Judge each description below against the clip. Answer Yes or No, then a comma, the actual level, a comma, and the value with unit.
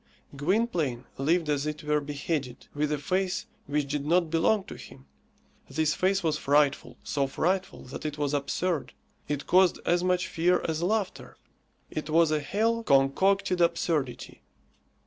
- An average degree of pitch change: Yes, average, 3.9 semitones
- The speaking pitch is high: No, medium, 155 Hz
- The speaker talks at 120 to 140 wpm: No, average, 150 wpm